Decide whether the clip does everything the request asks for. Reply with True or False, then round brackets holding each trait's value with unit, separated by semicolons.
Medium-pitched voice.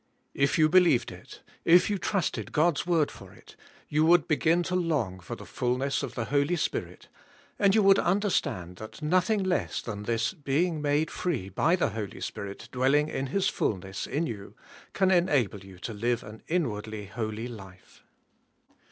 True (145 Hz)